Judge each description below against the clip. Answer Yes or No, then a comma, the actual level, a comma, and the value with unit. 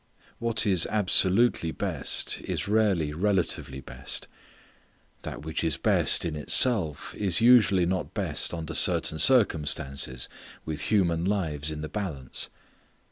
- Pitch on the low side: Yes, very low, 85 Hz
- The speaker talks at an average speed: No, slow, 125 wpm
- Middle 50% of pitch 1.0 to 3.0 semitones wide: No, average, 5.2 semitones